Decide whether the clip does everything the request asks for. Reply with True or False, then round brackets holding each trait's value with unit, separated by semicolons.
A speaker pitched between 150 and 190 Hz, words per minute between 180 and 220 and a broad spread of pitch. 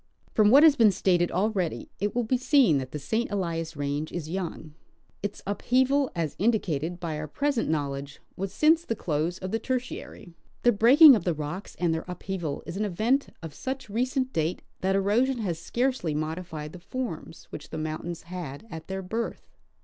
True (185 Hz; 185 wpm; 6.6 semitones)